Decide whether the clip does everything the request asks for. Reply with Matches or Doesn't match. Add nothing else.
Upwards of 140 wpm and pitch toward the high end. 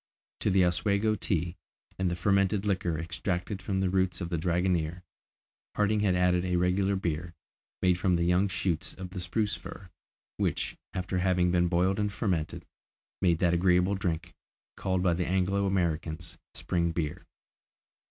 Doesn't match